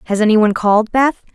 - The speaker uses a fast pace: No, average, 180 wpm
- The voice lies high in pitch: Yes, high, 220 Hz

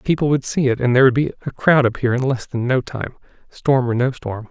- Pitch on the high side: No, low, 130 Hz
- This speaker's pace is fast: Yes, fast, 265 wpm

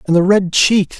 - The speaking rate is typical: No, fast, 240 wpm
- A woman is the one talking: No, male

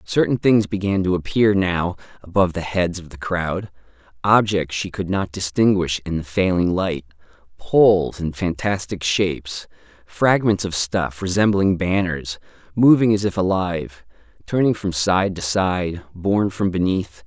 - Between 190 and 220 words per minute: No, average, 140 wpm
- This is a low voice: Yes, very low, 90 Hz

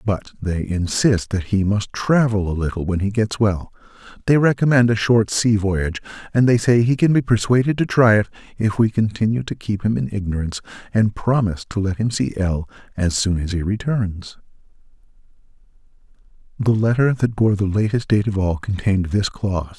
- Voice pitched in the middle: No, low, 105 Hz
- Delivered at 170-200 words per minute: Yes, average, 180 wpm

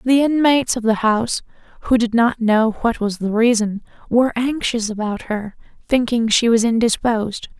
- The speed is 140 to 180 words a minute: Yes, average, 165 wpm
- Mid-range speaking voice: No, high, 230 Hz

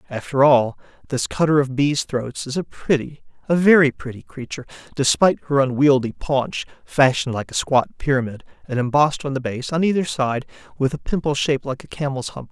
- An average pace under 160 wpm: No, average, 185 wpm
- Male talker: Yes, male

